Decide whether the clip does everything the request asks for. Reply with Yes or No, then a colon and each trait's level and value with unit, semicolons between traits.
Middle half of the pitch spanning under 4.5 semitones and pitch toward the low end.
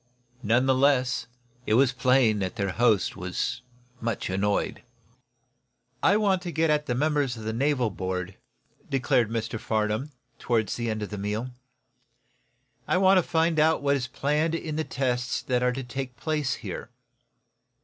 No: average, 5.0 semitones; low, 125 Hz